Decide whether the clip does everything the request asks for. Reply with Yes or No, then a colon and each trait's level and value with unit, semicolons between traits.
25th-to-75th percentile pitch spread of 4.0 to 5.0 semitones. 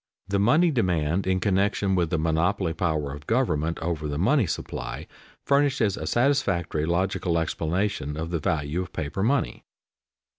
Yes: average, 4.4 semitones